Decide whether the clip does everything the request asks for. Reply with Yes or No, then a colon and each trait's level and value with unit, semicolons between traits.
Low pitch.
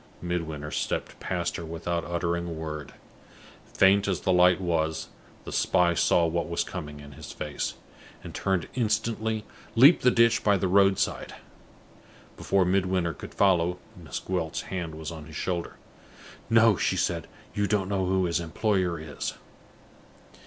Yes: very low, 90 Hz